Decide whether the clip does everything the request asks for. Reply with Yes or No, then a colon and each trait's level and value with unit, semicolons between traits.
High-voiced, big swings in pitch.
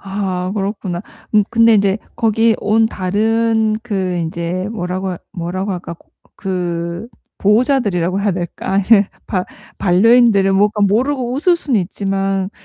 No: high, 200 Hz; average, 3.4 semitones